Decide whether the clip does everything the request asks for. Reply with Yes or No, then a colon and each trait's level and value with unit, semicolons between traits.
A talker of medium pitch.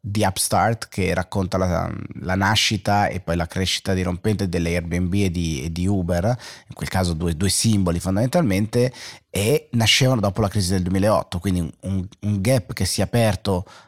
No: very low, 95 Hz